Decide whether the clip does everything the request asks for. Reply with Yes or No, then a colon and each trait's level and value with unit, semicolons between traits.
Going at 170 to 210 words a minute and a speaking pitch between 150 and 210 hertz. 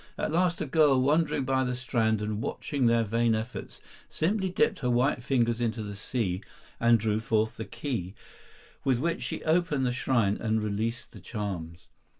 No: average, 175 wpm; low, 120 Hz